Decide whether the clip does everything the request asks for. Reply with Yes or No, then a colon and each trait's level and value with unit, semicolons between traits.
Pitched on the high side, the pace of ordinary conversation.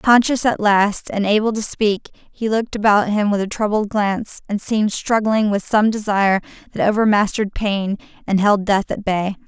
Yes: high, 210 Hz; average, 185 wpm